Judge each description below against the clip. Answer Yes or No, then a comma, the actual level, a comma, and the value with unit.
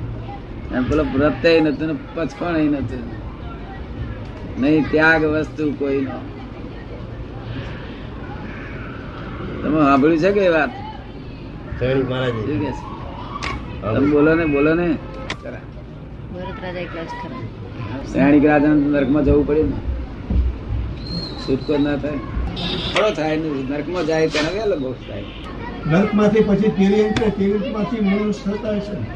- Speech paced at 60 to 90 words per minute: Yes, average, 80 wpm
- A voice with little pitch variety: No, average, 4.4 semitones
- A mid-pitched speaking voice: Yes, medium, 145 Hz